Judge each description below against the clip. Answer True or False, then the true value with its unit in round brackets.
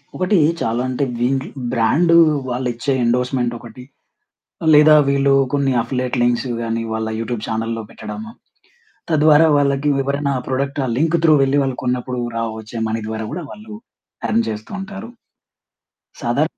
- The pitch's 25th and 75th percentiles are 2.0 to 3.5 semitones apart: False (4.0 semitones)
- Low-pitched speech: True (130 Hz)